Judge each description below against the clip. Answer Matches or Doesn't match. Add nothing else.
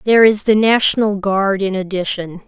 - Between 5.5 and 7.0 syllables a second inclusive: Doesn't match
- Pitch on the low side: Doesn't match